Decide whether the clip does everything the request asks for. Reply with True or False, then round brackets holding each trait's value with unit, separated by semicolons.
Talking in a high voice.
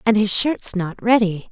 True (210 Hz)